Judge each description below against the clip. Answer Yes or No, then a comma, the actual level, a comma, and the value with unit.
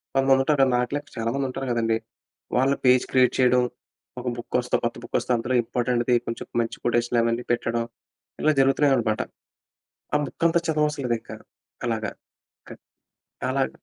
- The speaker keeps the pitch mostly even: Yes, narrow, 2.3 semitones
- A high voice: No, low, 125 Hz